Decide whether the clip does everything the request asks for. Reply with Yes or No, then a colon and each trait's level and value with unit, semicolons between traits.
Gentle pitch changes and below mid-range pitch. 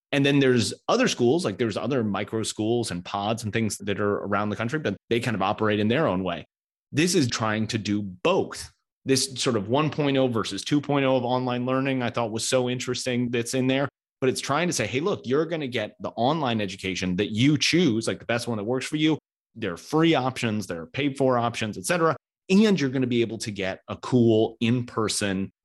No: average, 3.8 semitones; low, 120 Hz